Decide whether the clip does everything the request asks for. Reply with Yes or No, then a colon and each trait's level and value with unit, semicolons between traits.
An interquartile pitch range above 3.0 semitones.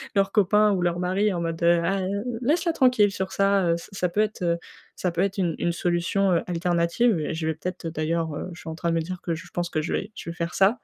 No: average, 2.7 semitones